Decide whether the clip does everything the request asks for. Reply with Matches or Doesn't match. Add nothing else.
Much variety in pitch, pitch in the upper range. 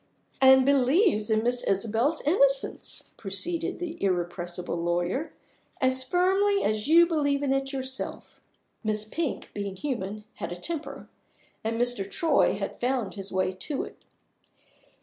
Matches